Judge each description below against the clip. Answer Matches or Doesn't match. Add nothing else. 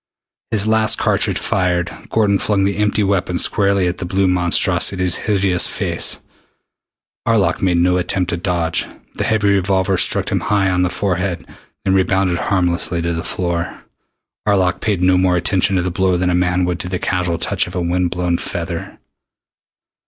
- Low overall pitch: Matches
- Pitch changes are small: Matches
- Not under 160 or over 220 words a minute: Matches